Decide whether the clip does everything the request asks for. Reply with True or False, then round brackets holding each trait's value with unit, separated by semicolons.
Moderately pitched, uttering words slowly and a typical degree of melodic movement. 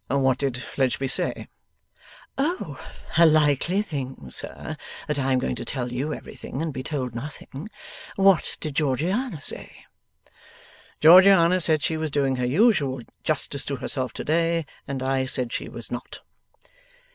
False (145 Hz; 150 wpm; 4.0 semitones)